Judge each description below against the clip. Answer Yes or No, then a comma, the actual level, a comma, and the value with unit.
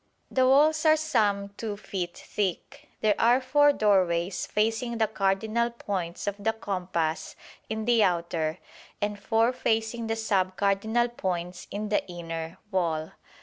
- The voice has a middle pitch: No, high, 210 Hz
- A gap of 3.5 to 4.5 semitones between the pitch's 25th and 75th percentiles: Yes, average, 4.0 semitones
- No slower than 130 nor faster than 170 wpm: Yes, average, 145 wpm